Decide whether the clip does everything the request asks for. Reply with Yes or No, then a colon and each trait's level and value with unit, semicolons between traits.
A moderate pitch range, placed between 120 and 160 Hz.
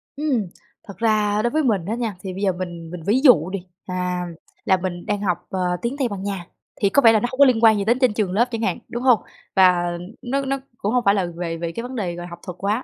No: average, 4.7 semitones; high, 205 Hz